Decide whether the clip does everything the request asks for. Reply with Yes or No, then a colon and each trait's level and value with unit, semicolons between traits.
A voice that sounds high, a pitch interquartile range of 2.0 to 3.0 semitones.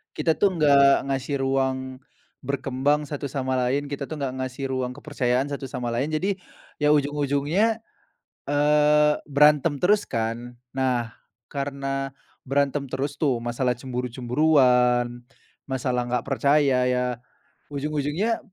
No: low, 135 Hz; average, 2.7 semitones